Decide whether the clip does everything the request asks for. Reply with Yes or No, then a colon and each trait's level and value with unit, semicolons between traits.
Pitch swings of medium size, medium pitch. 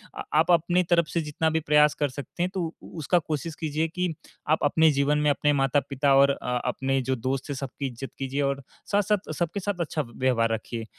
Yes: average, 3.3 semitones; medium, 150 Hz